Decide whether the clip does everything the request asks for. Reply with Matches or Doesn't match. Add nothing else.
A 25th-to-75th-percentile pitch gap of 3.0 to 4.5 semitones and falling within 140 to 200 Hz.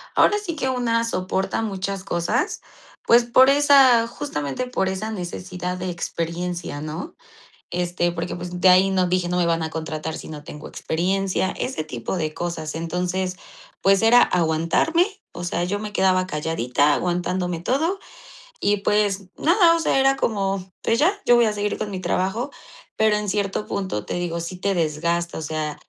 Matches